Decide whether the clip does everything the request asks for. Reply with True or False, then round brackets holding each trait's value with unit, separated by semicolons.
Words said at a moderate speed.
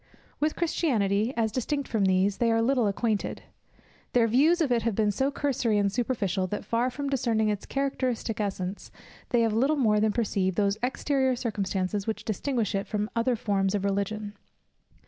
True (175 wpm)